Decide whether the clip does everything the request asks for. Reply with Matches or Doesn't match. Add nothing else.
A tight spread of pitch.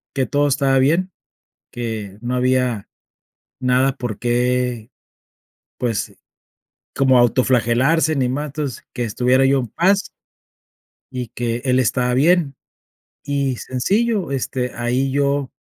Matches